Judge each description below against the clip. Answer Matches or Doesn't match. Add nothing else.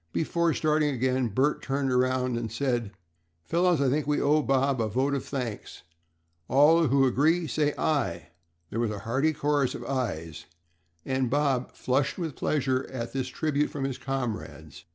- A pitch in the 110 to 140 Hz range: Matches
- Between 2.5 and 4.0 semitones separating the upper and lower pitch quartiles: Matches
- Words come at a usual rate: Matches